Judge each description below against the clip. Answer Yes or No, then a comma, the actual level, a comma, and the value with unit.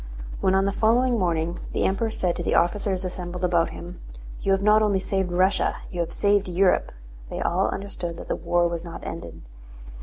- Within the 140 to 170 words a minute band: No, average, 195 wpm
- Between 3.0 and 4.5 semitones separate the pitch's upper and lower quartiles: No, narrow, 2.4 semitones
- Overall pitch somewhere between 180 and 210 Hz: Yes, medium, 185 Hz